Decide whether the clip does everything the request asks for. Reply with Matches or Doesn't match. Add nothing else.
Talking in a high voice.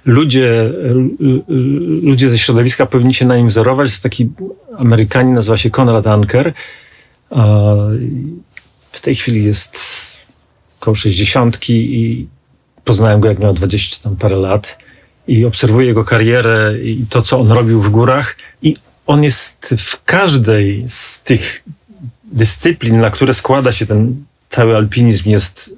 Doesn't match